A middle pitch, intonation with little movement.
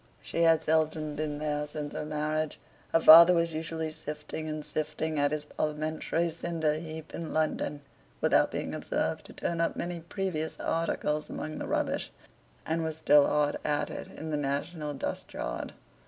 Yes: medium, 155 Hz; narrow, 1.3 semitones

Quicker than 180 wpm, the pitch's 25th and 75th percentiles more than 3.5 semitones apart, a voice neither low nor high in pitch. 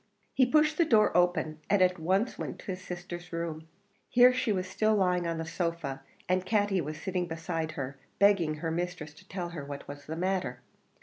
No: average, 200 wpm; average, 3.2 semitones; medium, 175 Hz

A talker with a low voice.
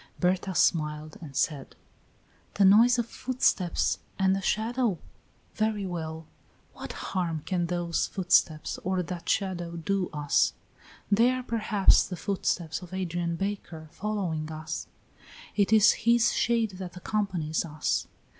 No: medium, 185 Hz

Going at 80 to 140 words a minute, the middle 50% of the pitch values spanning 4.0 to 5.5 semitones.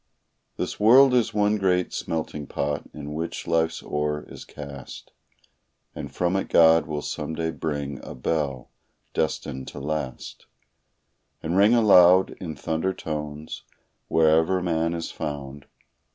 No: slow, 135 wpm; average, 3.6 semitones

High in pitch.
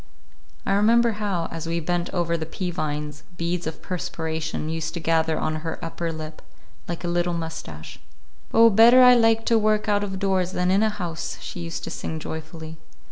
No: medium, 170 Hz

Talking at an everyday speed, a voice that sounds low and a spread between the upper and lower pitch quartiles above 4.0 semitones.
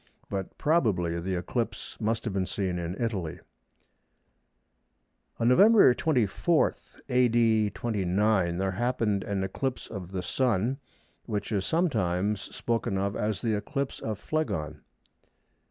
No: slow, 120 wpm; low, 105 Hz; average, 4.4 semitones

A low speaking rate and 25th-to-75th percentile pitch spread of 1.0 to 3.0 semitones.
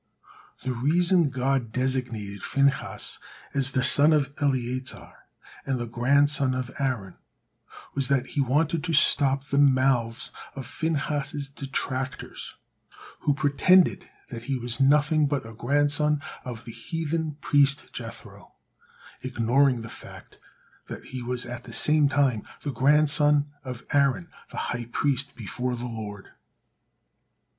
Yes: slow, 130 wpm; average, 2.7 semitones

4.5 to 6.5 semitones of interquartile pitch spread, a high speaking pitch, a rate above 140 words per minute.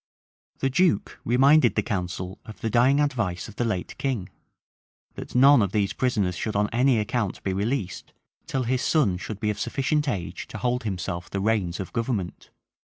No: average, 5.0 semitones; low, 110 Hz; average, 180 wpm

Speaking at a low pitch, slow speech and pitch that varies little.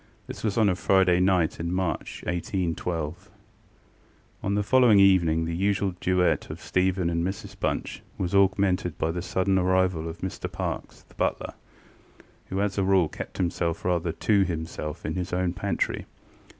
No: very low, 90 Hz; average, 165 wpm; narrow, 2.3 semitones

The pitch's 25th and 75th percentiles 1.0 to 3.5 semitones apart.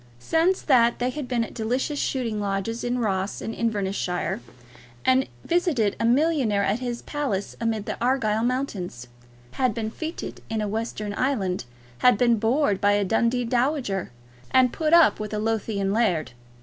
No: average, 3.9 semitones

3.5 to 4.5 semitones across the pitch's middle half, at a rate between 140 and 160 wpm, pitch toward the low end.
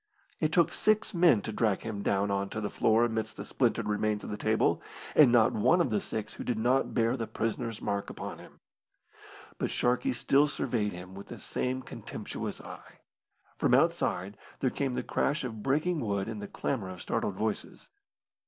No: average, 4.0 semitones; average, 190 wpm; low, 110 Hz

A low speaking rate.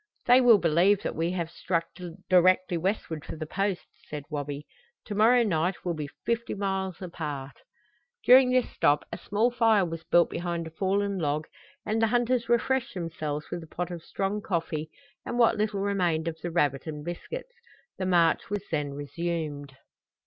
No: average, 175 wpm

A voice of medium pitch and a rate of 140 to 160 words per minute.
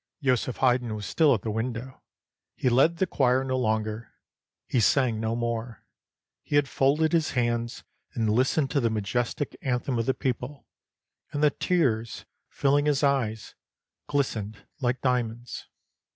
No: low, 125 Hz; average, 150 wpm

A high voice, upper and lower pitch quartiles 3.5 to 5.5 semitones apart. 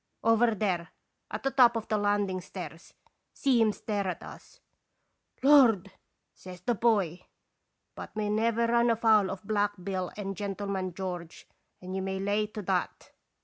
No: high, 205 Hz; average, 3.1 semitones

